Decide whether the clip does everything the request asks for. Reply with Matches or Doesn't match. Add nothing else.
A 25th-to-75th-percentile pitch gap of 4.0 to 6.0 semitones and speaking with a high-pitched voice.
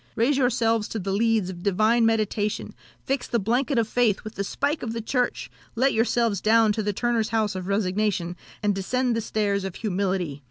Doesn't match